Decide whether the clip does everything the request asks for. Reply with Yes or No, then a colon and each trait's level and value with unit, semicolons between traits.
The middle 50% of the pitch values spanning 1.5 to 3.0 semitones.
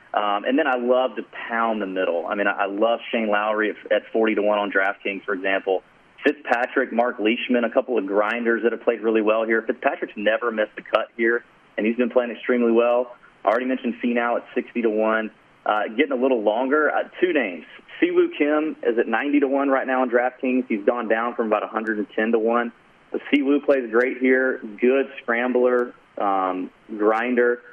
Yes: average, 2.7 semitones